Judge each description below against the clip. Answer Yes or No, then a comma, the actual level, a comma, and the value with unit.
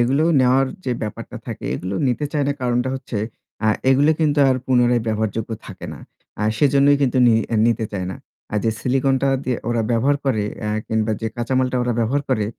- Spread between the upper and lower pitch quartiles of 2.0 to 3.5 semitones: Yes, average, 3.1 semitones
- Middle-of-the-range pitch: No, low, 125 Hz